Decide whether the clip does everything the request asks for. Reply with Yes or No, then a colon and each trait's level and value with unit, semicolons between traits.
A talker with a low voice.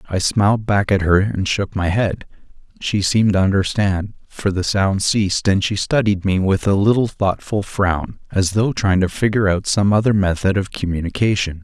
Yes: low, 100 Hz